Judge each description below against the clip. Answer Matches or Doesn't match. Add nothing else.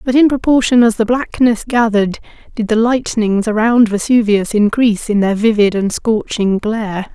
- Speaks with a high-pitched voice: Matches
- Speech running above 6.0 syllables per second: Doesn't match